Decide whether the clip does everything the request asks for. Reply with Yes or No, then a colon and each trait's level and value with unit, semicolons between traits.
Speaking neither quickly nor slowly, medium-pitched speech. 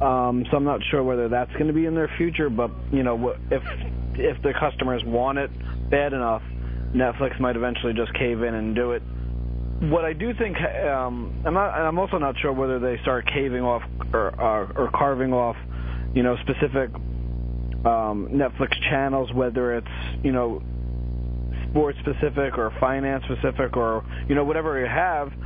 No: average, 175 wpm; low, 125 Hz